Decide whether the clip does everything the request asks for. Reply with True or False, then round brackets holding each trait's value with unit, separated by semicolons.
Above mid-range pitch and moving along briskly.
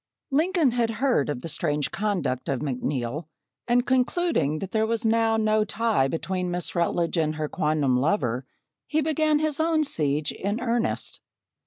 False (205 Hz; 160 wpm)